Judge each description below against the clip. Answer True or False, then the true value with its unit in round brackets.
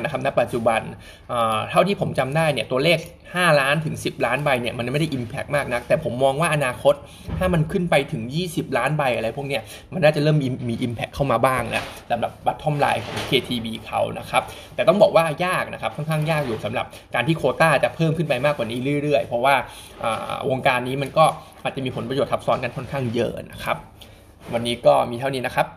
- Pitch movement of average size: True (4.7 semitones)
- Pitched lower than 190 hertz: True (135 Hz)